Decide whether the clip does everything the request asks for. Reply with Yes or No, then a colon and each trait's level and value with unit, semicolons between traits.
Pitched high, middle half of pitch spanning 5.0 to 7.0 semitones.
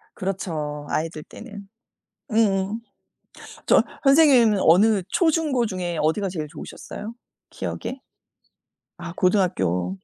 Yes: high, 195 Hz; wide, 5.6 semitones